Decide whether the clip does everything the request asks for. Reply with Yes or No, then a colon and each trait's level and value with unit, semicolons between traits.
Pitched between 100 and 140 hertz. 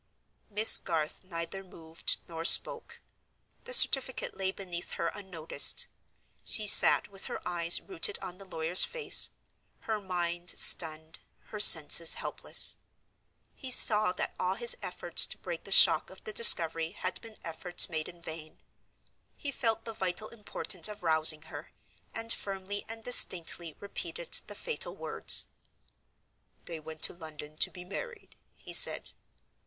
No: medium, 180 Hz